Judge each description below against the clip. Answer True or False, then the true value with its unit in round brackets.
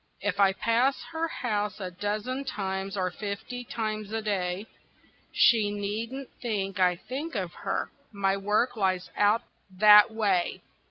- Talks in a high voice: True (205 Hz)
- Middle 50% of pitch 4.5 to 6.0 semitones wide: False (2.9 semitones)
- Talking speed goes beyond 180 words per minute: False (145 wpm)